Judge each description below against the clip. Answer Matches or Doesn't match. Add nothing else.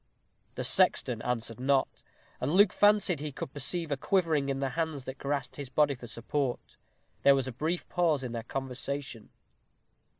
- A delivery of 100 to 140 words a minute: Doesn't match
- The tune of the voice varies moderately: Matches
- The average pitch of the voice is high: Doesn't match